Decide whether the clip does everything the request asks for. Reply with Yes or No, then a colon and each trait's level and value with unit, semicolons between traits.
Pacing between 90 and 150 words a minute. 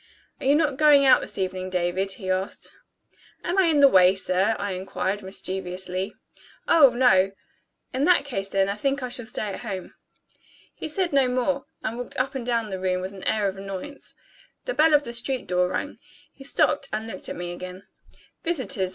No: average, 200 wpm